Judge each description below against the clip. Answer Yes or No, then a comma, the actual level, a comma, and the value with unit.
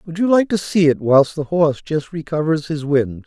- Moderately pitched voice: Yes, medium, 155 Hz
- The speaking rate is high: Yes, fast, 240 wpm